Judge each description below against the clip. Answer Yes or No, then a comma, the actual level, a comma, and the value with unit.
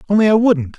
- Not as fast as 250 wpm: Yes, fast, 230 wpm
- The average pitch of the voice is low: No, high, 195 Hz